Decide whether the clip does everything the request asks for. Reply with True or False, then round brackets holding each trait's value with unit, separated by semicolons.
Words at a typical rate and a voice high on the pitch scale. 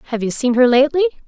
False (235 wpm; 270 Hz)